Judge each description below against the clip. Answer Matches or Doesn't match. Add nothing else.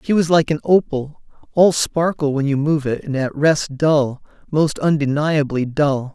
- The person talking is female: Doesn't match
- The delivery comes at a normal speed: Matches